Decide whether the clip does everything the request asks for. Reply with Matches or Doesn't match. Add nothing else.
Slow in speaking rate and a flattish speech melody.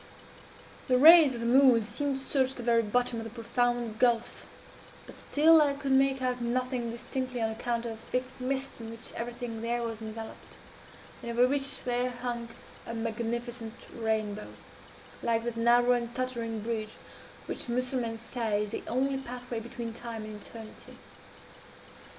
Doesn't match